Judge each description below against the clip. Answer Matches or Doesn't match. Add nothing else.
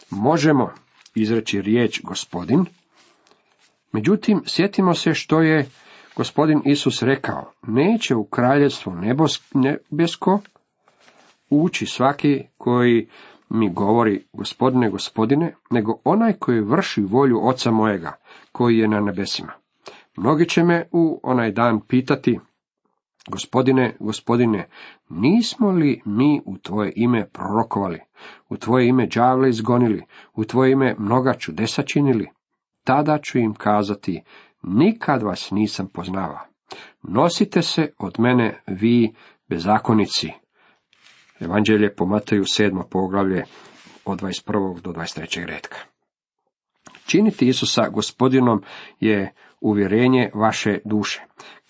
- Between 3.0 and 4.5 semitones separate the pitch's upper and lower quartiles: Doesn't match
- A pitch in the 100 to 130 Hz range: Matches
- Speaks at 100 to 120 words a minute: Matches